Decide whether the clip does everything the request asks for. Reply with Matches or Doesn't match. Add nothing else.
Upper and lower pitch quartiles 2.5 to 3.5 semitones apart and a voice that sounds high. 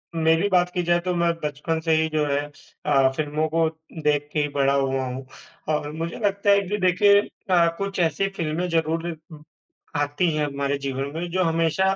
Doesn't match